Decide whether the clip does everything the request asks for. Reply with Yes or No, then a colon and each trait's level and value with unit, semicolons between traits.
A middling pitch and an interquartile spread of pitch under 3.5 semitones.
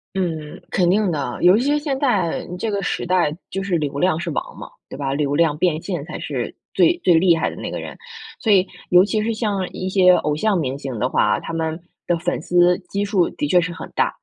No: medium, 180 Hz; average, 3.8 semitones